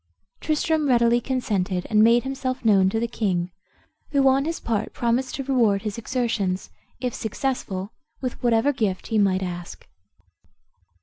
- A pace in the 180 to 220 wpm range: No, average, 145 wpm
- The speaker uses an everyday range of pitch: Yes, average, 4.6 semitones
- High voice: Yes, high, 230 Hz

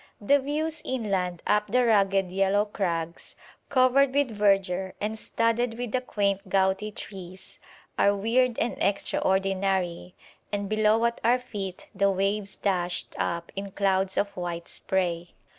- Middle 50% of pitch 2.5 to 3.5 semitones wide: Yes, average, 3.2 semitones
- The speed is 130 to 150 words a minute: Yes, average, 140 wpm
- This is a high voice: Yes, high, 200 Hz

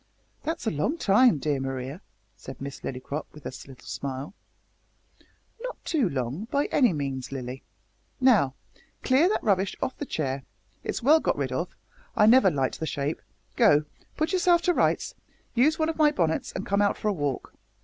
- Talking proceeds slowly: No, average, 180 wpm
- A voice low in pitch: No, medium, 185 Hz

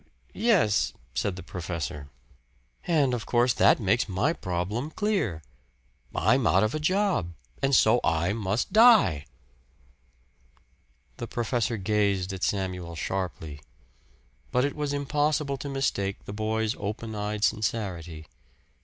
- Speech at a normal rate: No, slow, 125 wpm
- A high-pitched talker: No, low, 110 Hz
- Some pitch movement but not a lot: No, wide, 6.5 semitones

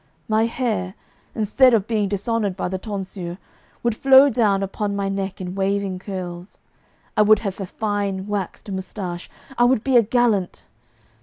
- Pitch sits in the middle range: No, high, 200 Hz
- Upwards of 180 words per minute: No, average, 160 wpm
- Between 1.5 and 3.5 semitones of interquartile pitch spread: Yes, average, 2.8 semitones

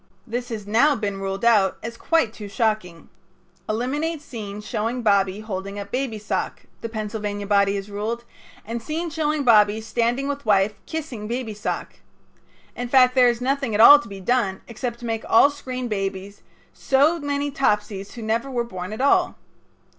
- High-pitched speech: Yes, high, 225 Hz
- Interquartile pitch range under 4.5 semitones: Yes, average, 3.8 semitones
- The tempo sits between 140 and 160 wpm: No, average, 175 wpm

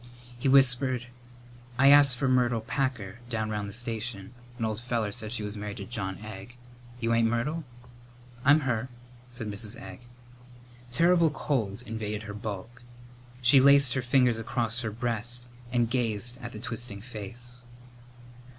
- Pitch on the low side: Yes, low, 120 Hz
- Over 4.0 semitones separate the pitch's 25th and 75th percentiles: No, average, 2.8 semitones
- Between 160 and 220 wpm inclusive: No, average, 150 wpm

